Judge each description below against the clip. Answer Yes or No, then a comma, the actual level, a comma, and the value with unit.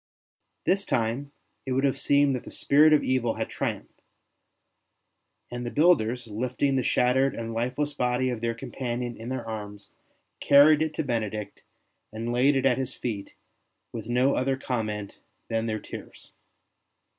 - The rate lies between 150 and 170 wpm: Yes, average, 155 wpm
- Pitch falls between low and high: No, low, 125 Hz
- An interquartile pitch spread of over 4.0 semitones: No, average, 3.1 semitones